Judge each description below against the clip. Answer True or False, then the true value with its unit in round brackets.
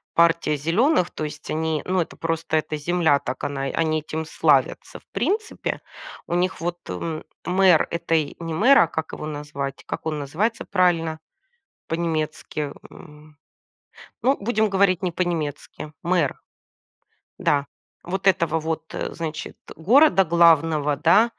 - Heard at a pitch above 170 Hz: False (165 Hz)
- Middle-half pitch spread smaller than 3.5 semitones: True (3.0 semitones)